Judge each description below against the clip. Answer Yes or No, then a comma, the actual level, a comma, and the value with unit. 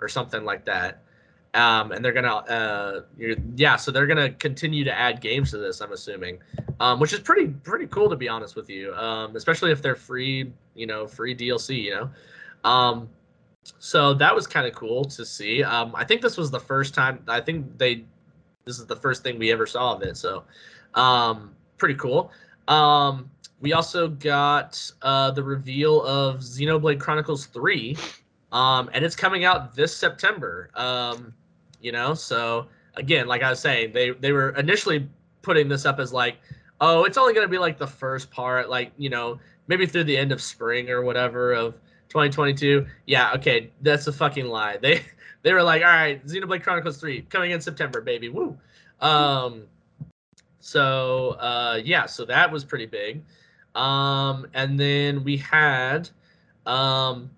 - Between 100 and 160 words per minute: No, average, 180 wpm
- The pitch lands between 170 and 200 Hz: No, medium, 140 Hz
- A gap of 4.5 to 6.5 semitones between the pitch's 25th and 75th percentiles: No, average, 3.9 semitones